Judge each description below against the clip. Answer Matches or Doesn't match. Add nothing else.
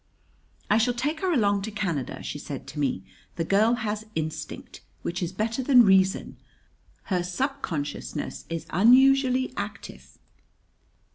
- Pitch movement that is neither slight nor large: Doesn't match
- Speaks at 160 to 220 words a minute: Doesn't match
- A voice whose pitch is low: Doesn't match